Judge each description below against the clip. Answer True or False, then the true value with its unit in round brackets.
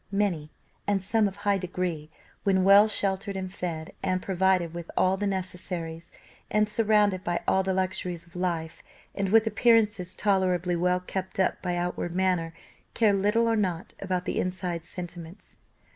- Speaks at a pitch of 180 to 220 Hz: True (185 Hz)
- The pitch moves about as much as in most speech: False (2.2 semitones)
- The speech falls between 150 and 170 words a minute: True (160 wpm)